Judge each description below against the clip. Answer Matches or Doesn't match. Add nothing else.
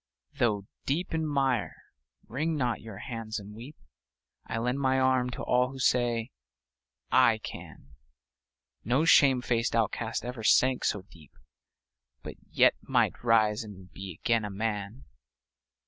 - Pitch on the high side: Doesn't match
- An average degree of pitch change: Matches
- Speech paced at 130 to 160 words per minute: Matches